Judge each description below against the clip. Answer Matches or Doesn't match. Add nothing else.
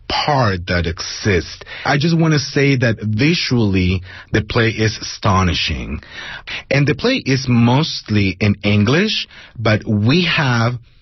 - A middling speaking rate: Doesn't match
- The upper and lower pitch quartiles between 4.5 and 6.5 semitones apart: Matches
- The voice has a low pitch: Matches